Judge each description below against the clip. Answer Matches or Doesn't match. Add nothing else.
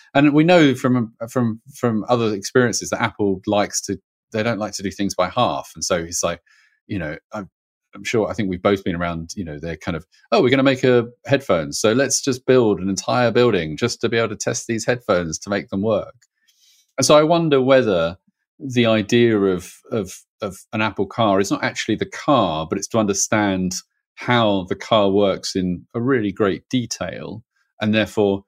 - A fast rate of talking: Matches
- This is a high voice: Doesn't match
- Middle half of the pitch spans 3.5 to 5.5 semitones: Matches